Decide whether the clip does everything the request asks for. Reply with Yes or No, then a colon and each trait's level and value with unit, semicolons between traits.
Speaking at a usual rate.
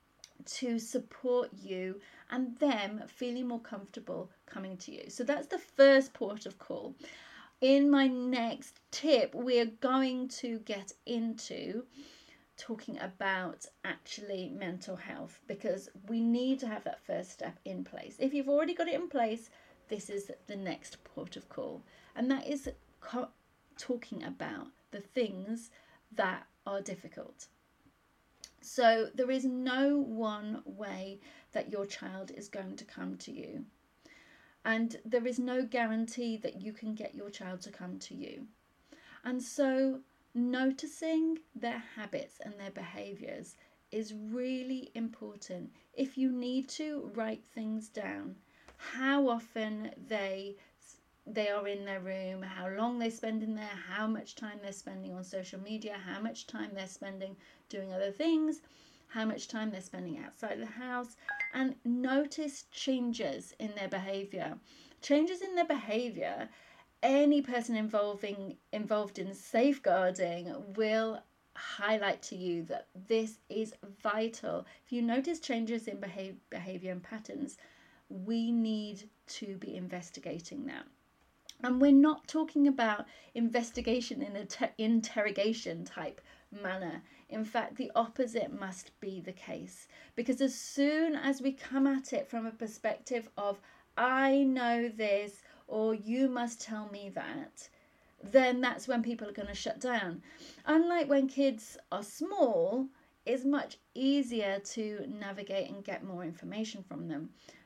Yes: average, 145 wpm